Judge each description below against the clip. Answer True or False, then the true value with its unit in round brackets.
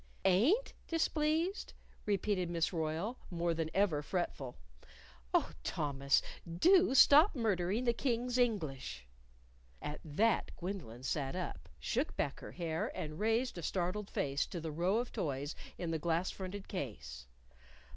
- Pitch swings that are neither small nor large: False (6.7 semitones)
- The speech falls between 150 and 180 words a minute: False (135 wpm)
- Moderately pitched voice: True (180 Hz)